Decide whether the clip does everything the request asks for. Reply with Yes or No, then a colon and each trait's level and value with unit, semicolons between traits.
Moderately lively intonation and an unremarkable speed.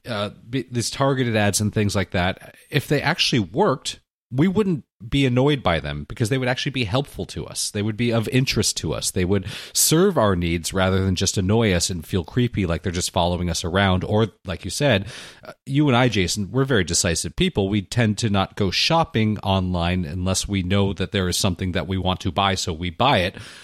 No: average, 4.6 semitones; fast, 220 wpm